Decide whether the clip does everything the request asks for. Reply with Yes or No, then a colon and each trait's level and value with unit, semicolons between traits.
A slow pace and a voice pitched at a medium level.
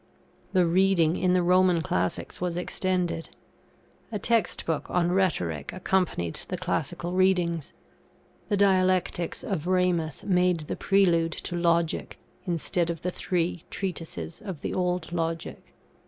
Yes: slow, 130 wpm; medium, 175 Hz